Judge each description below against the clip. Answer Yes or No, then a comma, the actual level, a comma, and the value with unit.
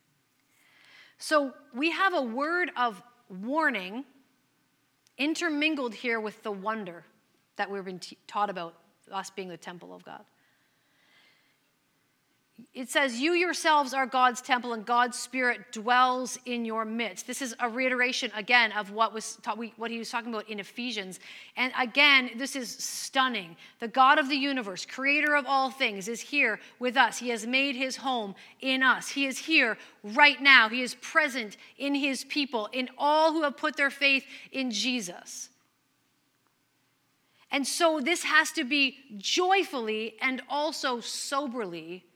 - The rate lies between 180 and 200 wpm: No, average, 155 wpm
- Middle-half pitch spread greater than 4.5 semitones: No, average, 4.1 semitones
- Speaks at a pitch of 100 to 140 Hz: No, very high, 250 Hz